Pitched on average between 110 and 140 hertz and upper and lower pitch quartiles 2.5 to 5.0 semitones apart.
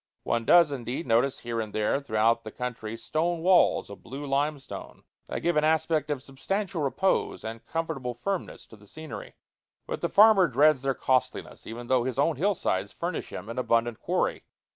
No: low, 135 Hz; wide, 5.5 semitones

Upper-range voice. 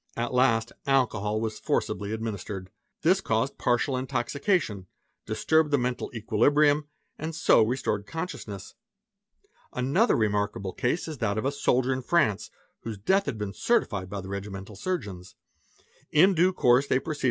No: low, 115 Hz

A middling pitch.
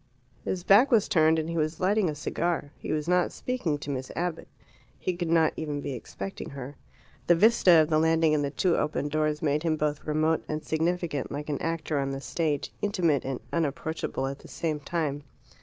Yes: medium, 155 Hz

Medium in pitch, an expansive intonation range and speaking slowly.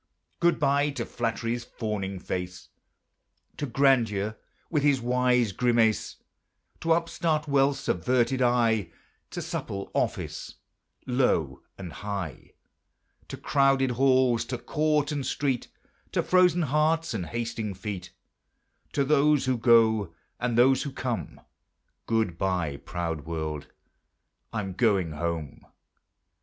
No: low, 120 Hz; wide, 5.9 semitones; slow, 115 wpm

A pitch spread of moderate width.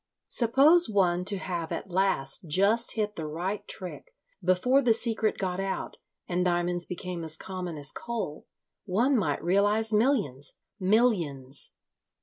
Yes: average, 4.2 semitones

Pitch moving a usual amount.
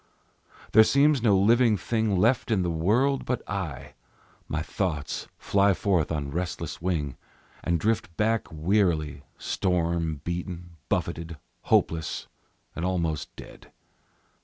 Yes: average, 4.6 semitones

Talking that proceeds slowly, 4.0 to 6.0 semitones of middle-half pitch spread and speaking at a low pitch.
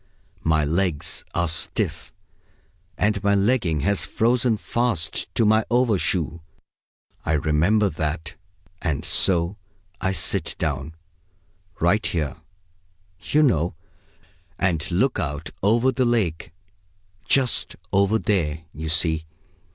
Yes: slow, 110 wpm; wide, 5.4 semitones; very low, 90 Hz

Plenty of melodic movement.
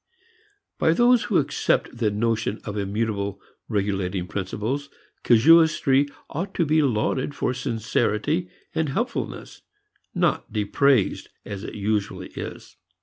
Yes: wide, 5.8 semitones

